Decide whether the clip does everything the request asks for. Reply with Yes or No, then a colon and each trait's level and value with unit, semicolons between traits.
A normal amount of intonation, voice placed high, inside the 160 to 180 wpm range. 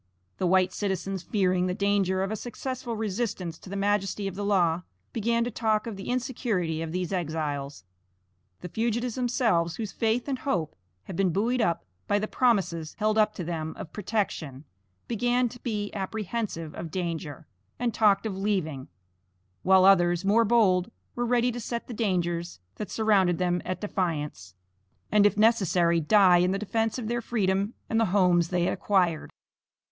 Yes: average, 4.1 semitones; high, 195 Hz; average, 170 wpm